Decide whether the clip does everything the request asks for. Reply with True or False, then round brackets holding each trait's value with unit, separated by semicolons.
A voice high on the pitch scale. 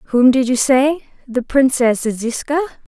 True (260 Hz)